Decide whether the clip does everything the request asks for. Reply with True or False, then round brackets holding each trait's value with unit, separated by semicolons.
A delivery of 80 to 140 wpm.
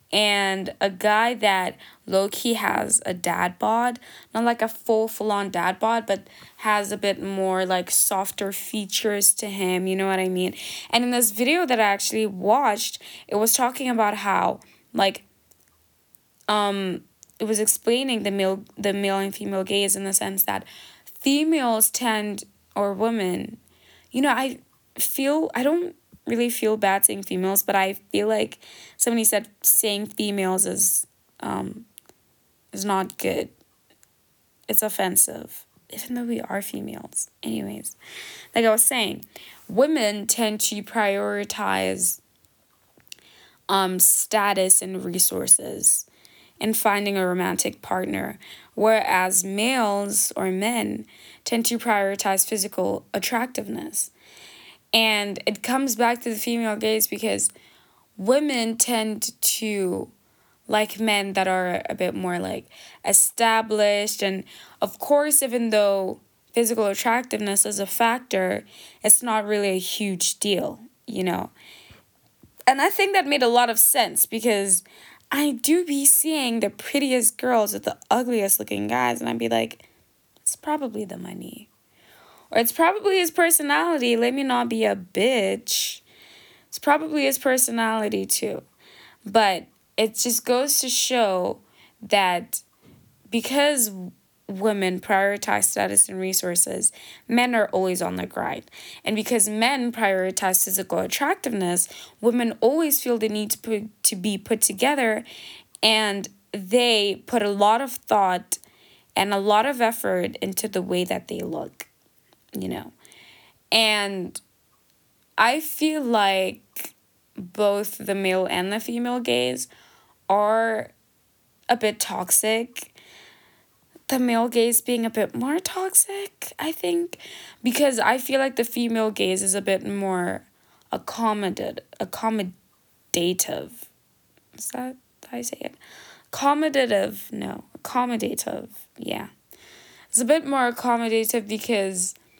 True (135 wpm)